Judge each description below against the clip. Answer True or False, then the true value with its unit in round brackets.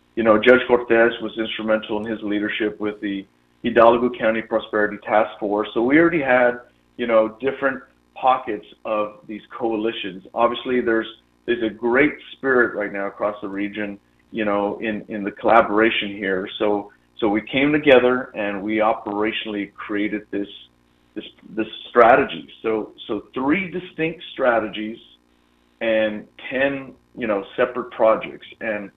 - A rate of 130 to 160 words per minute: True (145 wpm)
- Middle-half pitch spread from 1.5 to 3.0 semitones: True (2.5 semitones)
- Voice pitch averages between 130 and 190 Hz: False (110 Hz)